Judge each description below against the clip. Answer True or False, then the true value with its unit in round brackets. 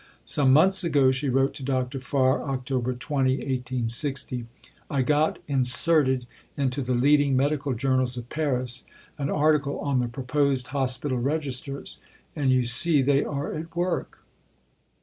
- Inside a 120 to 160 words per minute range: True (140 wpm)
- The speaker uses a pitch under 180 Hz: True (135 Hz)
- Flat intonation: True (2.2 semitones)